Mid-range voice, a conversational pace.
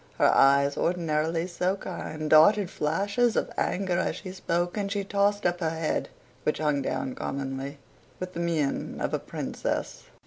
Yes: medium, 170 Hz; average, 165 wpm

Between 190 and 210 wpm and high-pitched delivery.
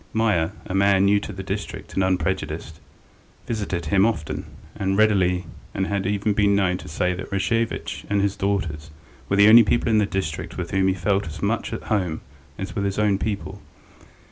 No: average, 195 wpm; very low, 95 Hz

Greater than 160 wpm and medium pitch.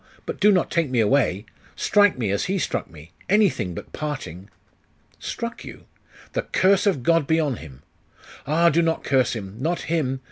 Yes: average, 180 wpm; medium, 150 Hz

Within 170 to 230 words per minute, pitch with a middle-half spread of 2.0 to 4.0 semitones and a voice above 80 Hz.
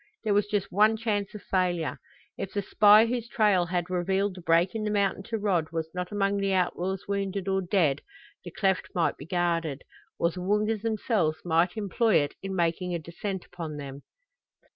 Yes: average, 190 wpm; average, 3.0 semitones; high, 190 Hz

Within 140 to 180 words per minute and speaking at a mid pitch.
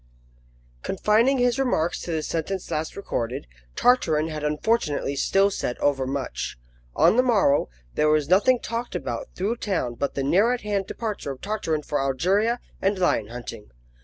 Yes: average, 160 wpm; medium, 180 Hz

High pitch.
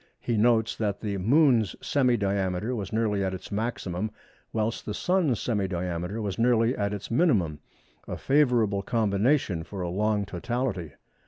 No: low, 105 Hz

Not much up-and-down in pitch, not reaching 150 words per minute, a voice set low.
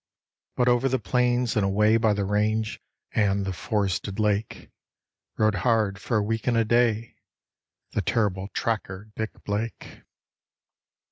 Yes: narrow, 2.2 semitones; average, 140 wpm; low, 110 Hz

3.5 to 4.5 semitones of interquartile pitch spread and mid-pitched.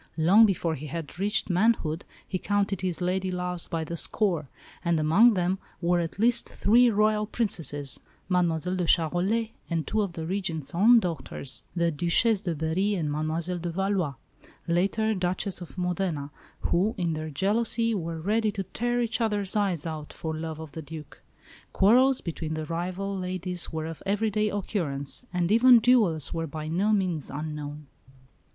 Yes: average, 4.2 semitones; medium, 180 Hz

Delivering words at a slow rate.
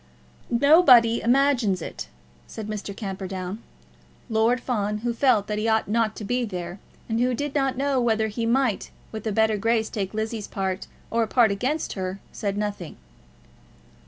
No: average, 165 wpm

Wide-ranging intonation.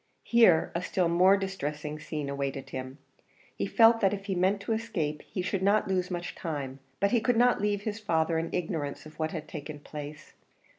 No: average, 4.8 semitones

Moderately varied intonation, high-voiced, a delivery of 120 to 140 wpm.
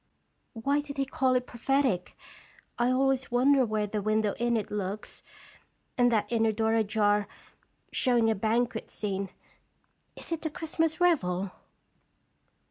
Yes: average, 4.1 semitones; high, 230 Hz; slow, 135 wpm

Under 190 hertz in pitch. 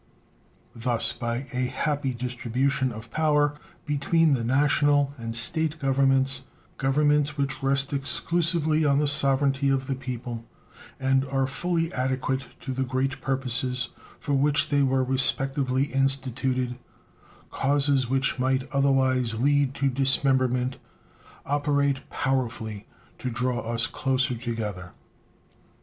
Yes: low, 135 Hz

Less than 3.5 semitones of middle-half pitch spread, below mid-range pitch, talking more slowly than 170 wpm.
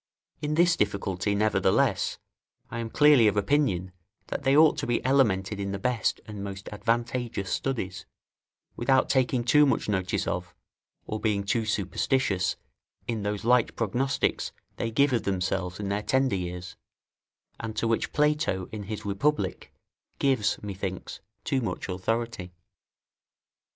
No: average, 4.7 semitones; low, 110 Hz; average, 140 wpm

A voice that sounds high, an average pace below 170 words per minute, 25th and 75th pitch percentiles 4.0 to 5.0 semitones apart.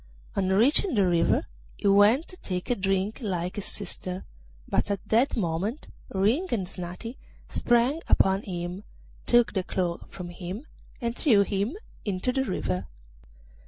Yes: high, 200 Hz; average, 150 wpm; average, 4.4 semitones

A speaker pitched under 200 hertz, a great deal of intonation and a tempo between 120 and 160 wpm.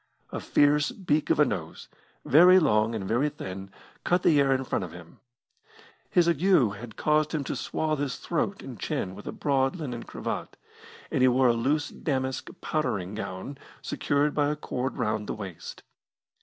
No: low, 135 Hz; wide, 5.8 semitones; average, 180 wpm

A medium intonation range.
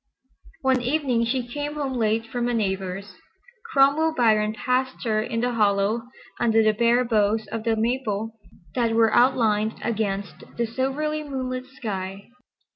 Yes: average, 3.1 semitones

